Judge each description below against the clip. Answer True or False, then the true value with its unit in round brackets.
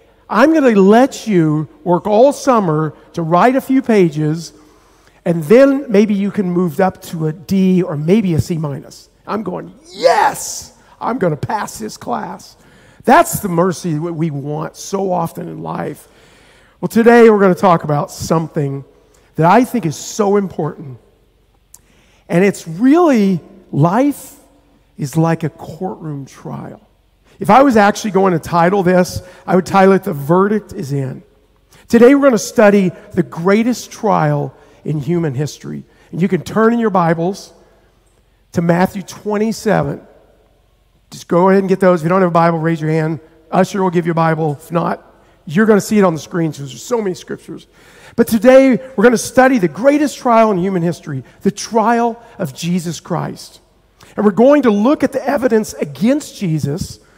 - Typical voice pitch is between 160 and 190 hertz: True (185 Hz)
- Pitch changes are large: False (4.8 semitones)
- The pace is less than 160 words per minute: False (180 wpm)